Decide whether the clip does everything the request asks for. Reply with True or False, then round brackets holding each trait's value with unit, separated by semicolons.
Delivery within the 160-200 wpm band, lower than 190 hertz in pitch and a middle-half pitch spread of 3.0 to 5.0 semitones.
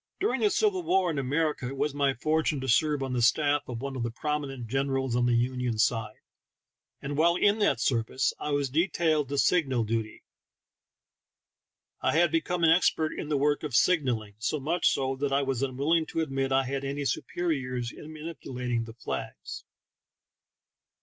True (185 wpm; 140 Hz; 3.7 semitones)